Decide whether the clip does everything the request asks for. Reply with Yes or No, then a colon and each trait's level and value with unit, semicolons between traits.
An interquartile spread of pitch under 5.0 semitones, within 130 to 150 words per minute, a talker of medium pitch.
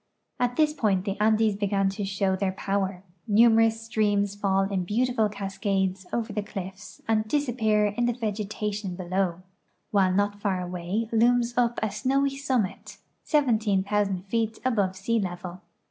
No: average, 2.8 semitones; average, 145 wpm; high, 205 Hz